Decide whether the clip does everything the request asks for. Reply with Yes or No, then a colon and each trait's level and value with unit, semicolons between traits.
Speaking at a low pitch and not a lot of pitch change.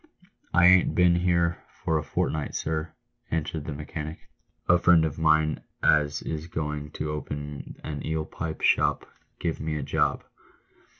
Yes: very low, 80 Hz; narrow, 1.6 semitones